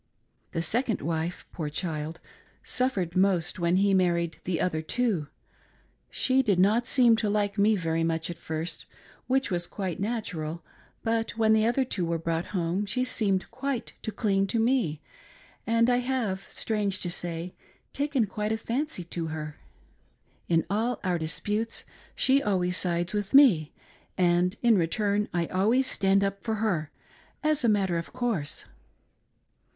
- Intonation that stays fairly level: No, average, 4.9 semitones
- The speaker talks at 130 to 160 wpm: Yes, average, 155 wpm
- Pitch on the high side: Yes, high, 195 Hz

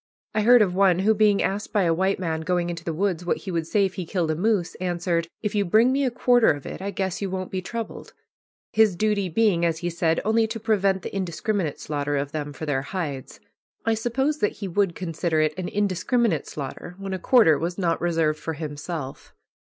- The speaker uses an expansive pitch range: No, average, 4.1 semitones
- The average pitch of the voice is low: No, medium, 185 Hz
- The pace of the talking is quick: Yes, fast, 225 wpm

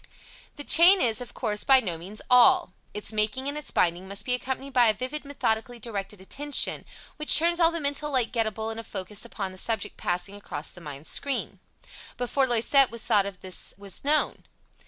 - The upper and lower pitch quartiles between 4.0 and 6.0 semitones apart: Yes, wide, 5.5 semitones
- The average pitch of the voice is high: Yes, high, 225 Hz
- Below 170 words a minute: No, average, 200 wpm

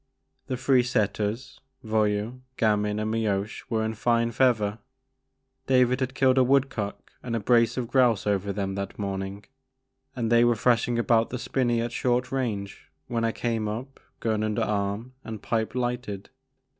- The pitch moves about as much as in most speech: Yes, average, 3.0 semitones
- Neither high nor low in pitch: No, low, 115 Hz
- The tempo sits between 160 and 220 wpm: Yes, average, 170 wpm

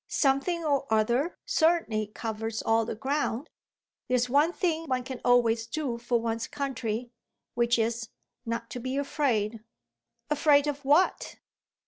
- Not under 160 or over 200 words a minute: No, slow, 135 wpm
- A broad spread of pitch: No, average, 4.0 semitones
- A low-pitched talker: No, very high, 250 Hz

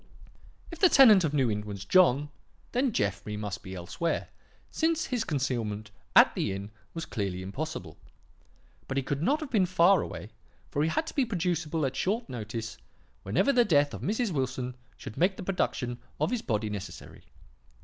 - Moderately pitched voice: Yes, medium, 145 Hz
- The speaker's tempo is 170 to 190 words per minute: Yes, average, 180 wpm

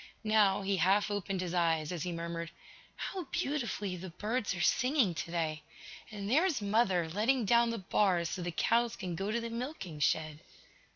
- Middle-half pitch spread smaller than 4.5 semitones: No, average, 5.1 semitones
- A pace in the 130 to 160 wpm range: No, average, 175 wpm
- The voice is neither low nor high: No, high, 195 Hz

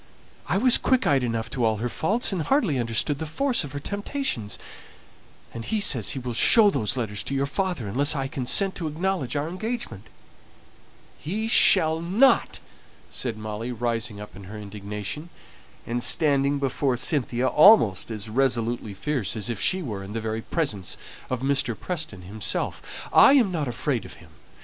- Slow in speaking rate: No, average, 175 wpm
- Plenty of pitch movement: Yes, wide, 7.3 semitones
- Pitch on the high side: No, low, 135 Hz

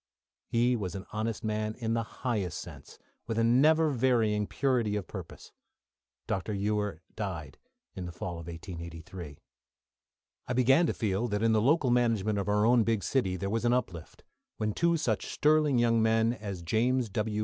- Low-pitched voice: Yes, low, 110 Hz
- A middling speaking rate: Yes, average, 175 wpm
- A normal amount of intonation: Yes, average, 3.8 semitones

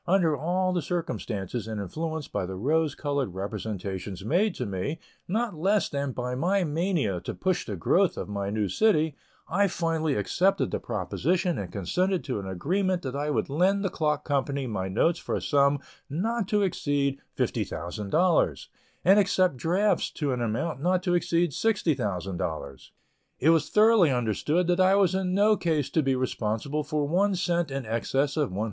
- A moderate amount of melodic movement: No, wide, 7.4 semitones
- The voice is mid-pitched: Yes, medium, 150 Hz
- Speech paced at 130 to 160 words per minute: No, average, 175 wpm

